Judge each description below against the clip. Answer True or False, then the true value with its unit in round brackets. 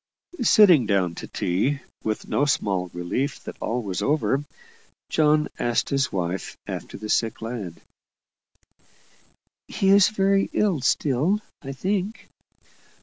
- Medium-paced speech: False (125 wpm)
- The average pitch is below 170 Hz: True (135 Hz)